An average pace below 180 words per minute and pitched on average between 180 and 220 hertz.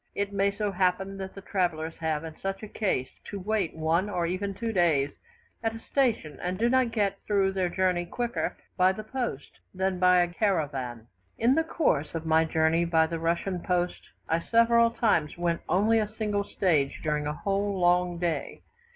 No: average, 185 wpm; medium, 185 Hz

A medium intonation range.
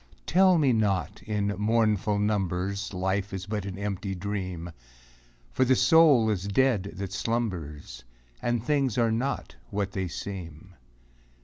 Yes: average, 3.5 semitones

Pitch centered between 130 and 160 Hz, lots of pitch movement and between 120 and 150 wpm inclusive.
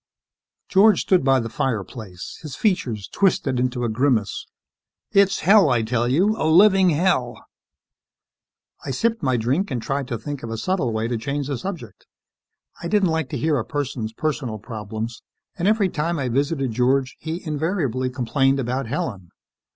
No: low, 135 Hz; wide, 5.9 semitones; average, 165 wpm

